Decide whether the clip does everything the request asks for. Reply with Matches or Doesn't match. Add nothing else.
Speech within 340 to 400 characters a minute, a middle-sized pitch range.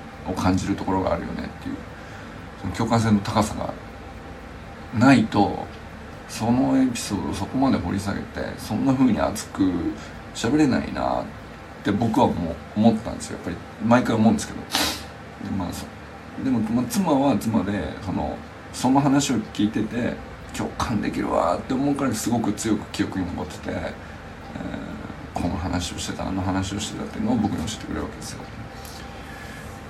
Doesn't match